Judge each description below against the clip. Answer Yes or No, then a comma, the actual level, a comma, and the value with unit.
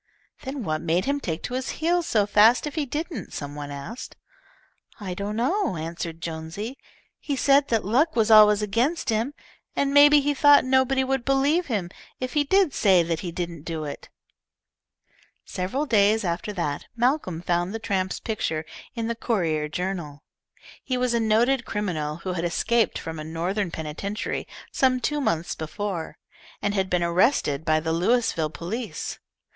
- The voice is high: Yes, high, 210 Hz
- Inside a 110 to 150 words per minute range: No, average, 170 wpm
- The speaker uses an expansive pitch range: Yes, wide, 7.4 semitones